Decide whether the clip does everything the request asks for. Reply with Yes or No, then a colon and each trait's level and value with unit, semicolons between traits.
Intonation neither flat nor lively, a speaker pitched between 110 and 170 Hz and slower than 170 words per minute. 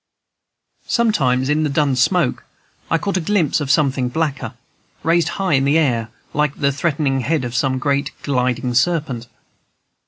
Yes: average, 3.9 semitones; medium, 140 Hz; average, 155 wpm